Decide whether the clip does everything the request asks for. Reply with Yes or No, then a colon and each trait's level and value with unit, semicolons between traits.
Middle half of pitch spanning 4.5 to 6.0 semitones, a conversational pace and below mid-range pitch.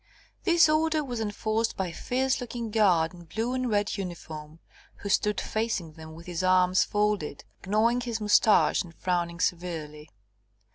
No: average, 5.1 semitones; average, 155 wpm; high, 205 Hz